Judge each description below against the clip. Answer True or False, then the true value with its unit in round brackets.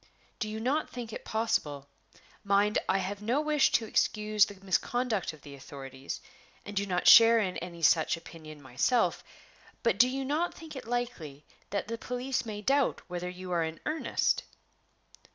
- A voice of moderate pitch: False (205 Hz)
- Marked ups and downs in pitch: True (6.1 semitones)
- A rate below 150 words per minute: False (170 wpm)